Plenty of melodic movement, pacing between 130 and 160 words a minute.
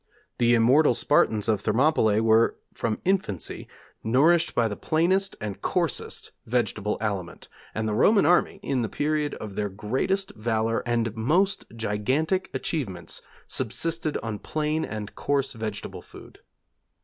Yes: wide, 6.4 semitones; slow, 135 wpm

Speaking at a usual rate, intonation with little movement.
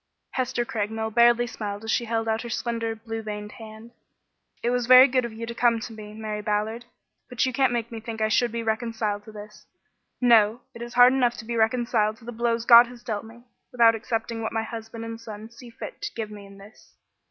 No: fast, 230 wpm; narrow, 1.5 semitones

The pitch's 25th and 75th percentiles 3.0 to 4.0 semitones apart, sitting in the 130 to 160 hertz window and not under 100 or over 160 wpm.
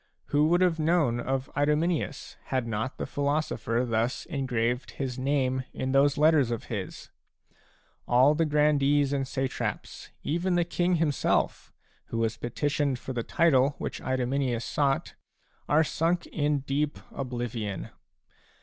Yes: average, 3.3 semitones; medium, 140 Hz; average, 140 wpm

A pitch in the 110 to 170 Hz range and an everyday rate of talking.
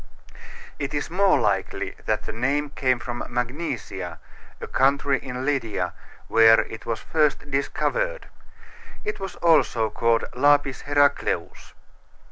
No: low, 135 Hz; slow, 120 wpm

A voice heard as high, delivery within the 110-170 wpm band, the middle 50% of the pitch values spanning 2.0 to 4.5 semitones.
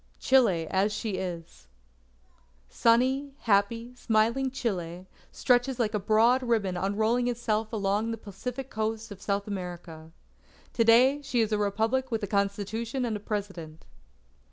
Yes: high, 220 Hz; average, 140 wpm; average, 3.3 semitones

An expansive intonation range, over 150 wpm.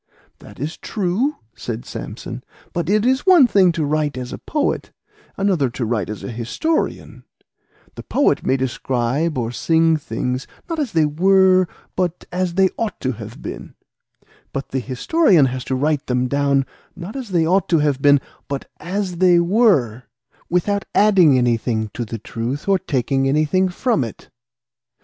Yes: wide, 6.6 semitones; average, 165 wpm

